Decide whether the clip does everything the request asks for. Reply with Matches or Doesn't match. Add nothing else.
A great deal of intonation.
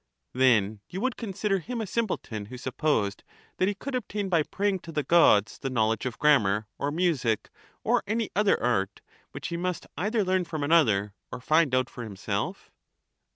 Matches